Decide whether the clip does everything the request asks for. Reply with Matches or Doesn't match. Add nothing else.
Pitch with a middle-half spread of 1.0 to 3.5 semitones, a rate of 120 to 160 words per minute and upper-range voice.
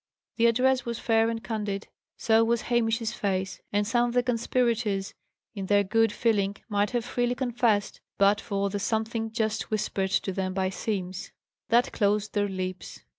Doesn't match